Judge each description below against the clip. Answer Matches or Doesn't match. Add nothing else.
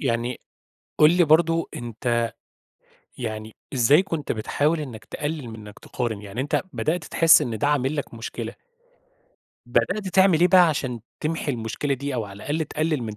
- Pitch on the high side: Doesn't match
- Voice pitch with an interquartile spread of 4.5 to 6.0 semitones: Matches